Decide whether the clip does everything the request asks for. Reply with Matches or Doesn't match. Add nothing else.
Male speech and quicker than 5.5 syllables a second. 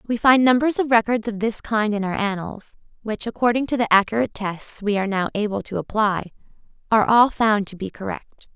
Doesn't match